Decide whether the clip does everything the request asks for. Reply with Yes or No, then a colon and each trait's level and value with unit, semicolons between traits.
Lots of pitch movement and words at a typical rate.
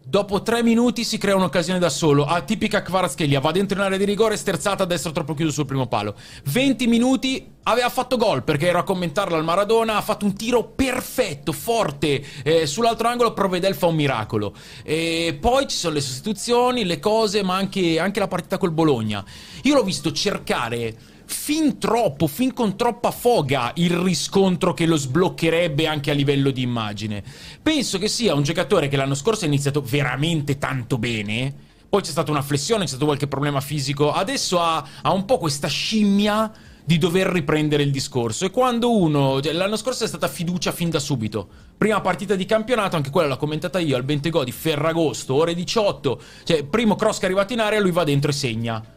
No: wide, 6.3 semitones; fast, 190 wpm